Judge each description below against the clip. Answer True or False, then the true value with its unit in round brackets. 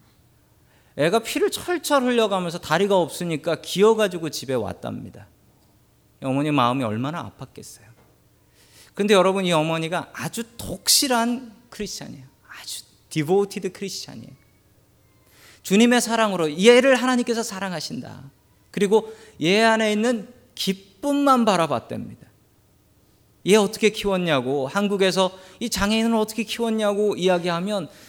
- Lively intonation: True (7.9 semitones)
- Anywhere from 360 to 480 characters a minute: False (305 characters per minute)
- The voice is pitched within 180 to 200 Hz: True (190 Hz)